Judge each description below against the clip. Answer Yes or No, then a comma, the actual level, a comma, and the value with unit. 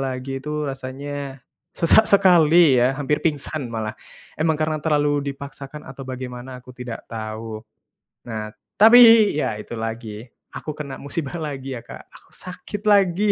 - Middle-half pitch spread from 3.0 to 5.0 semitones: Yes, average, 3.7 semitones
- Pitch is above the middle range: No, medium, 140 Hz